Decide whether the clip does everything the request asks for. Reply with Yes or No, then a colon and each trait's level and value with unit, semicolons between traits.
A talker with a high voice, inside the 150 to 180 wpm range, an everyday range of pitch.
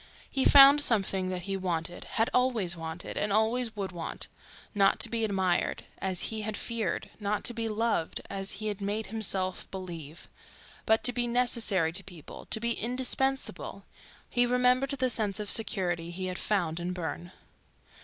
Yes: high, 205 Hz; average, 165 wpm; average, 4.4 semitones